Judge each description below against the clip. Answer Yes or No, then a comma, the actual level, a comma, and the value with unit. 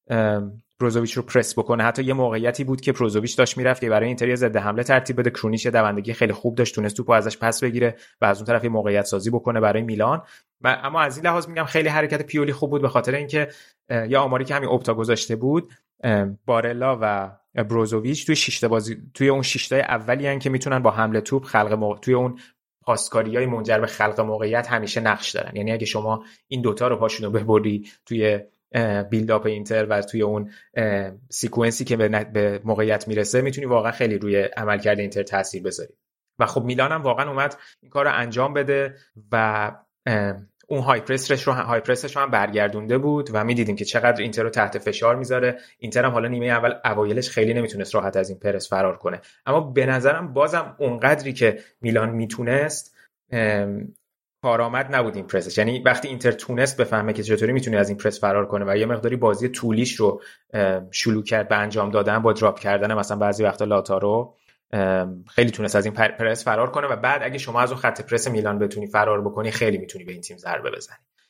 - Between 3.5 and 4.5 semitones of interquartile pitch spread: No, average, 3.1 semitones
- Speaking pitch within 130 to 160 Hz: No, low, 115 Hz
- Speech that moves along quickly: Yes, fast, 190 wpm